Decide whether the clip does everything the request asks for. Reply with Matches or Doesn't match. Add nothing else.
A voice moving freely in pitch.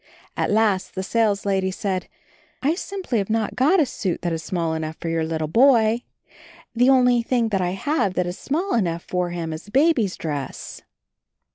Matches